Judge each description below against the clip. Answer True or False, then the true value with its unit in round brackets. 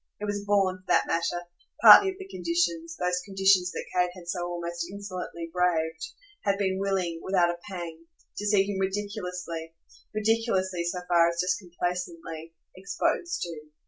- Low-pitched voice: False (185 Hz)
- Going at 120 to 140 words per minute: False (160 wpm)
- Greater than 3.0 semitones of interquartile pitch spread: False (2.7 semitones)